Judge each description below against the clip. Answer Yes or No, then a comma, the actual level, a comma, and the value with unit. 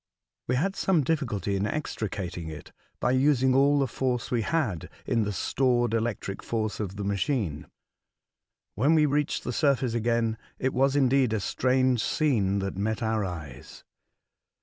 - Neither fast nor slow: Yes, average, 155 wpm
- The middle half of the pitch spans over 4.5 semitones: Yes, average, 4.9 semitones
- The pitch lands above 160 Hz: No, low, 120 Hz